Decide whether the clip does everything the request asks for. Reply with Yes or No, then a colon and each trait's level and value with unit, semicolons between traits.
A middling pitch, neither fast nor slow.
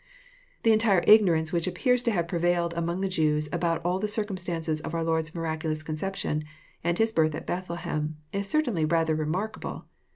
Yes: medium, 170 Hz; average, 175 wpm